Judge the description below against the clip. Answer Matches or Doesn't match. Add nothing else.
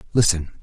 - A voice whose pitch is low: Matches